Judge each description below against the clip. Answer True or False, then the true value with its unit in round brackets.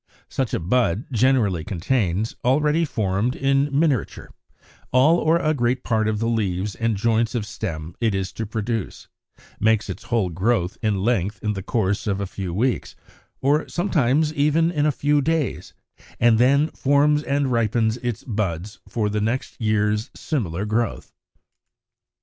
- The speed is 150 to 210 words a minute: True (155 wpm)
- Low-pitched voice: True (115 Hz)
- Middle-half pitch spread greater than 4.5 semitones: True (4.9 semitones)